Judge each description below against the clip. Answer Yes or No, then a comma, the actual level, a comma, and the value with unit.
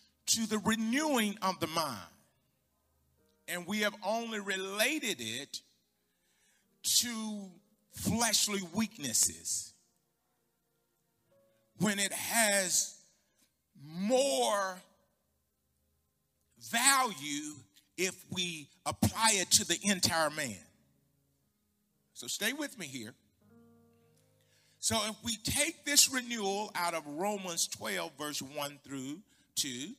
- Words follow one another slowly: Yes, slow, 95 wpm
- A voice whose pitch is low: No, high, 190 Hz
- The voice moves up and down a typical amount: No, wide, 8.3 semitones